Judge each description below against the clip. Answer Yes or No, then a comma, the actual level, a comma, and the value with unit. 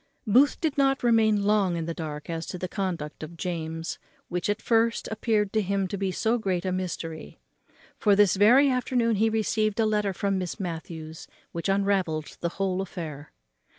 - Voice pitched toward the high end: Yes, high, 195 Hz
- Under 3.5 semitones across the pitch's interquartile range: No, average, 4.3 semitones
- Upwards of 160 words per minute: Yes, average, 185 wpm